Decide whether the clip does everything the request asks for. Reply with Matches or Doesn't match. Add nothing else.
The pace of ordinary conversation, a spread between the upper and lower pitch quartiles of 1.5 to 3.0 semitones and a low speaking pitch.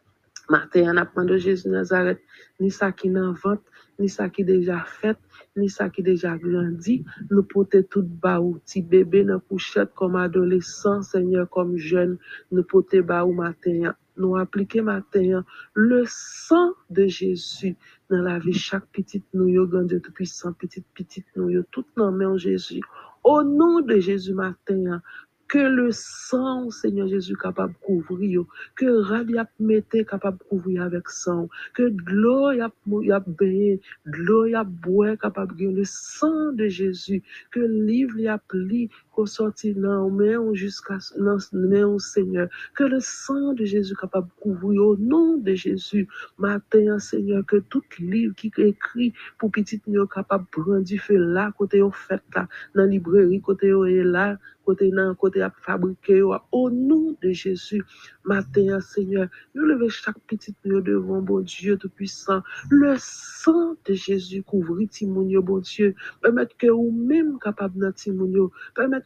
Doesn't match